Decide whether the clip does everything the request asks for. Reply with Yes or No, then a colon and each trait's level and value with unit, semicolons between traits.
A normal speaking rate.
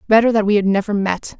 No: fast, 260 wpm